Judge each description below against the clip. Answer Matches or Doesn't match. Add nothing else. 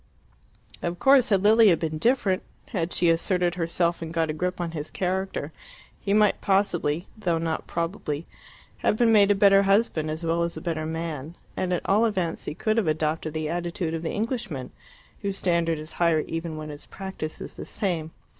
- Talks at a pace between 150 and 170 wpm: Doesn't match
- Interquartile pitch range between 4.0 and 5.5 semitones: Doesn't match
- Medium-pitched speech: Matches